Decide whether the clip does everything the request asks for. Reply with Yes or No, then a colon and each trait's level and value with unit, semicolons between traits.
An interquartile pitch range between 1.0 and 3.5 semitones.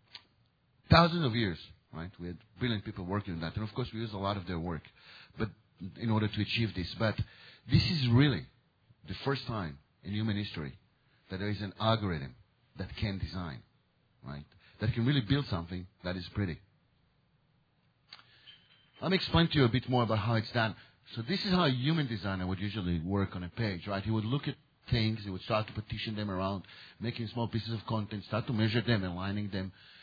No: average, 4.0 semitones